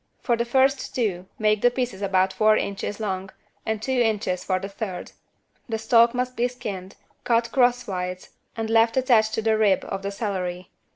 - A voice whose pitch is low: No, high, 220 Hz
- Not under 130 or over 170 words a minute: No, average, 180 wpm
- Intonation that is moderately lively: Yes, average, 3.7 semitones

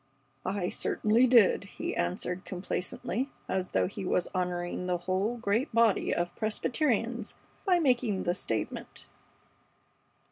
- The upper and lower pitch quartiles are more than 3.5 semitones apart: Yes, average, 4.6 semitones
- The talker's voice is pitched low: No, high, 200 Hz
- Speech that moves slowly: Yes, slow, 120 wpm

